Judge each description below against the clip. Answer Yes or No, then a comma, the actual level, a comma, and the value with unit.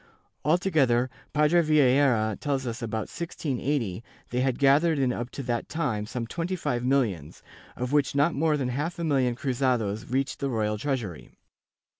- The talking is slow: No, average, 165 wpm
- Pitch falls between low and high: No, low, 130 Hz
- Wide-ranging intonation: No, average, 3.8 semitones